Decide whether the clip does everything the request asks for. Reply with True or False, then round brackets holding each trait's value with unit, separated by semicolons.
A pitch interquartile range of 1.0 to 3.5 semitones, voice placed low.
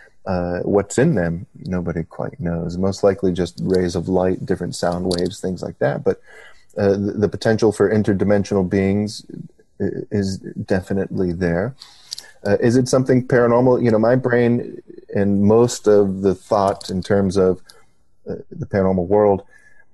True (2.9 semitones; 100 Hz)